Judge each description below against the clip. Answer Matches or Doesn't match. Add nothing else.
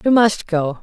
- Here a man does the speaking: Doesn't match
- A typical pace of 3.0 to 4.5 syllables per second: Matches